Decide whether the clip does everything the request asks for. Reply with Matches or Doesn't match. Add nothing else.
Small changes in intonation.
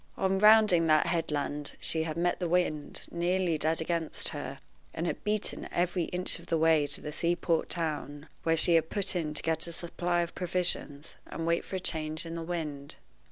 Matches